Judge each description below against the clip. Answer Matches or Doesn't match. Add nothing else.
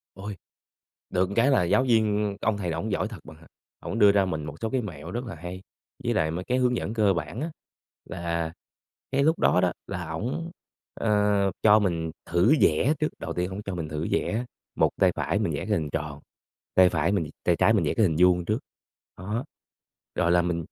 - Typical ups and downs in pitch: Matches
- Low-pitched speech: Matches